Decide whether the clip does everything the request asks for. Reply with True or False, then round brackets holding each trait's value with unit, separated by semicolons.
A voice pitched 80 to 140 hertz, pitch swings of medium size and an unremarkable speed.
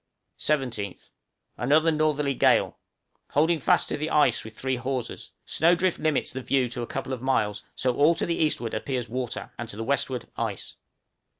True (135 Hz; 3.8 semitones; 180 wpm)